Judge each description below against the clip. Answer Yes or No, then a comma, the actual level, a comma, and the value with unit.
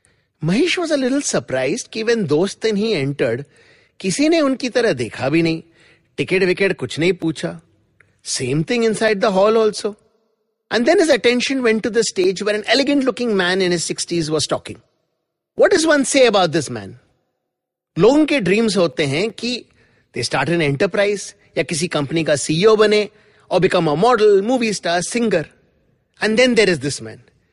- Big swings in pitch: Yes, wide, 5.8 semitones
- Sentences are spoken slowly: No, average, 155 wpm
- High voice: Yes, high, 200 Hz